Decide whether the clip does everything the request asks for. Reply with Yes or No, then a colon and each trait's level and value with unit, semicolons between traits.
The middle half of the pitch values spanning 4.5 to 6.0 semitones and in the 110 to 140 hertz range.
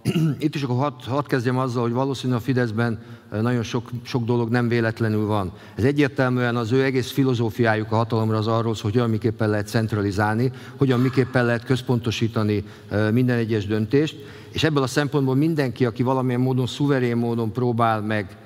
No: average, 2.8 semitones; low, 120 Hz